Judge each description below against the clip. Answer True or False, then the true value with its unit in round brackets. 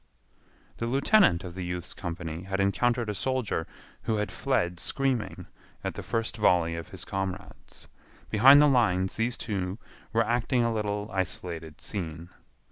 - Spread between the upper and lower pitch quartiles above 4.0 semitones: True (4.8 semitones)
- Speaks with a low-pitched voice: True (100 Hz)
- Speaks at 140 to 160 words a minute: True (150 wpm)